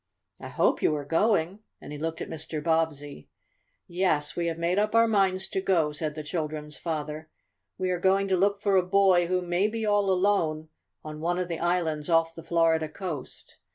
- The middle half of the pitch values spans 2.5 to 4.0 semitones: Yes, average, 3.3 semitones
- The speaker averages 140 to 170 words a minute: No, average, 200 wpm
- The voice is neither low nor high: Yes, medium, 170 Hz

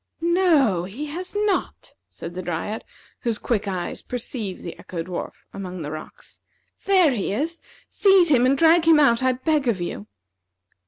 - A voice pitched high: Yes, high, 245 Hz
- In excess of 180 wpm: No, average, 165 wpm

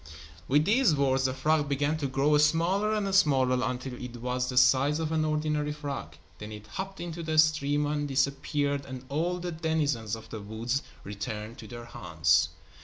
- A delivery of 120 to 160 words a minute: No, average, 180 wpm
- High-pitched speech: No, medium, 140 Hz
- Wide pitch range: No, average, 3.8 semitones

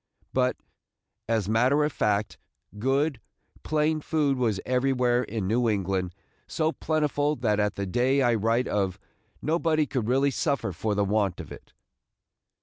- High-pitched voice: No, low, 125 Hz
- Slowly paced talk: No, average, 145 wpm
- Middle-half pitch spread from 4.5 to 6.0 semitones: Yes, average, 5.2 semitones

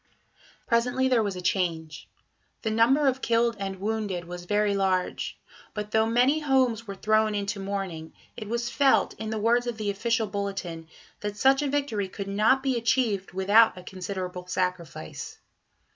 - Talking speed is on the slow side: No, average, 165 wpm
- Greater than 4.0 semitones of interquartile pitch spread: No, average, 3.7 semitones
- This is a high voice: Yes, high, 210 Hz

